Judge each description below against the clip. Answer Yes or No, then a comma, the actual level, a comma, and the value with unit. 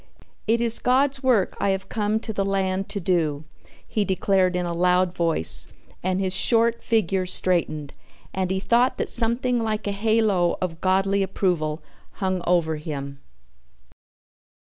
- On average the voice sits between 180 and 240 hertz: Yes, high, 190 Hz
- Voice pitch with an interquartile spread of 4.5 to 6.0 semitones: No, average, 3.7 semitones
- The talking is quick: No, average, 150 wpm